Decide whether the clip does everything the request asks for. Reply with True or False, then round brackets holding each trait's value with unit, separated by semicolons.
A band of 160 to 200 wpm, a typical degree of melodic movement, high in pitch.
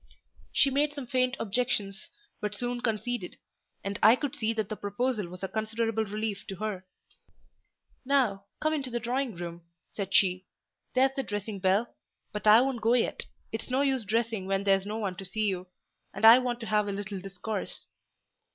True (185 wpm; 3.7 semitones; 220 Hz)